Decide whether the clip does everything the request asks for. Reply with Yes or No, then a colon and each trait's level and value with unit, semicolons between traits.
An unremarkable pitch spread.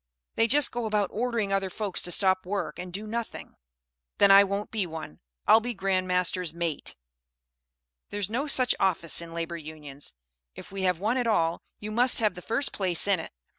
Yes: average, 3.7 semitones